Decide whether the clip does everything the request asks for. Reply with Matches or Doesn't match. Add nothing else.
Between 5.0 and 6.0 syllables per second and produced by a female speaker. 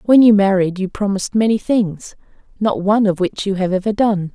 Matches